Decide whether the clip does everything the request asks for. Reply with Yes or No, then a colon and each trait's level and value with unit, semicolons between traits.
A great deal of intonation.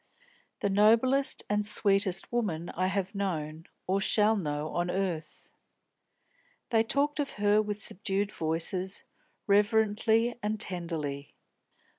No: average, 3.7 semitones